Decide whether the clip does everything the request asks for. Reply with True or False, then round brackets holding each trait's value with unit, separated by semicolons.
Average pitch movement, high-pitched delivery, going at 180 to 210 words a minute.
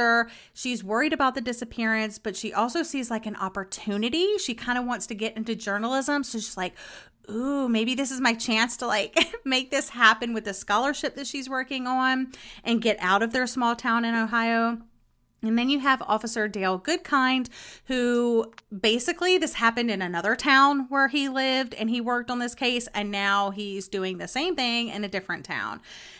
True (3.1 semitones; 235 Hz; 190 wpm)